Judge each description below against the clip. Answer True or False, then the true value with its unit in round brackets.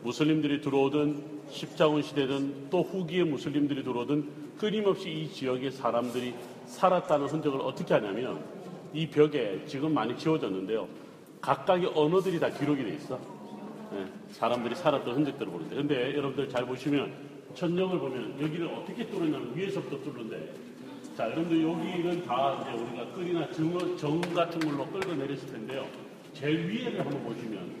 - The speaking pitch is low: False (150 Hz)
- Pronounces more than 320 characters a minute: True (365 characters per minute)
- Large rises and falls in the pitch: False (3.7 semitones)